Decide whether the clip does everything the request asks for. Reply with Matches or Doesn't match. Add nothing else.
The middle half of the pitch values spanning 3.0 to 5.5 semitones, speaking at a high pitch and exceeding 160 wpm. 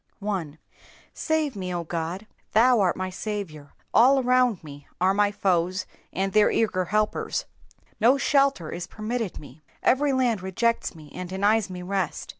Doesn't match